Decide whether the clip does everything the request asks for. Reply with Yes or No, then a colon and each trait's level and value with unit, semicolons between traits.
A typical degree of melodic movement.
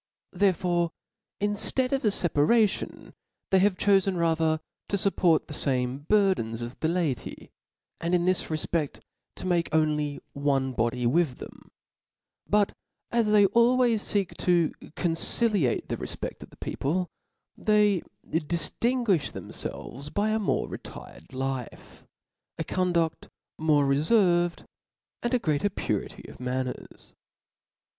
No: wide, 5.7 semitones